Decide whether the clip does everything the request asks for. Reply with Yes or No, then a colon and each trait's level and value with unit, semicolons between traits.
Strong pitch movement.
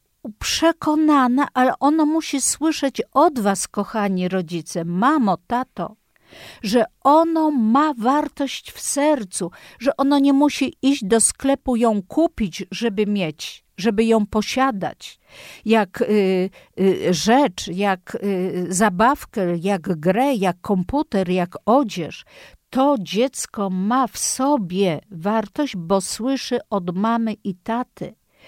Yes: wide, 5.9 semitones